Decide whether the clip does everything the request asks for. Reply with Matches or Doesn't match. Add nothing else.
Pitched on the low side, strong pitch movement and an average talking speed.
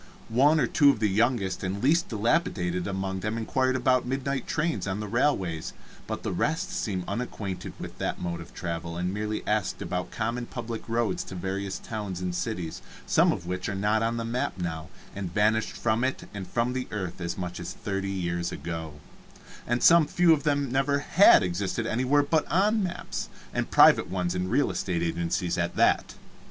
Matches